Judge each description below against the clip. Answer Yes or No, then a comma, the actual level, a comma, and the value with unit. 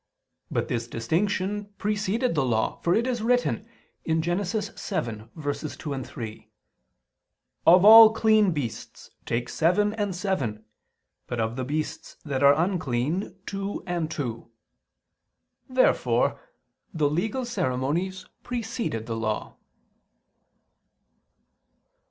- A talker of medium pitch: Yes, medium, 170 Hz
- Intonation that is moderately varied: No, wide, 8.1 semitones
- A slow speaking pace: Yes, slow, 105 wpm